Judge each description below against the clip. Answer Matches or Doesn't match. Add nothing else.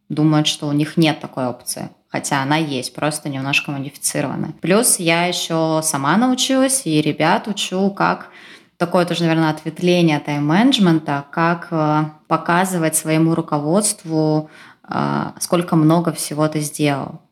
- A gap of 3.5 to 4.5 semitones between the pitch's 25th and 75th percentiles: Doesn't match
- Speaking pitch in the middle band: Matches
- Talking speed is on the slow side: Doesn't match